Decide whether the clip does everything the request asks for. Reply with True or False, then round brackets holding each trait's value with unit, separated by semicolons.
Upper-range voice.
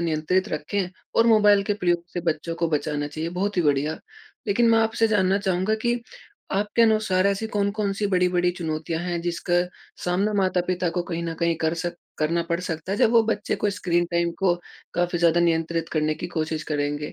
False (175 Hz)